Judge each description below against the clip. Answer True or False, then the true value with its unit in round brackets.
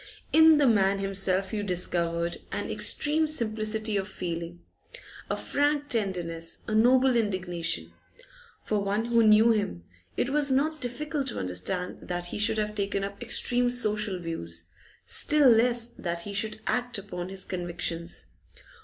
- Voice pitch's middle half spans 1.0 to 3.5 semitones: False (5.4 semitones)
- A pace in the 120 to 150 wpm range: True (145 wpm)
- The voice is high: True (210 Hz)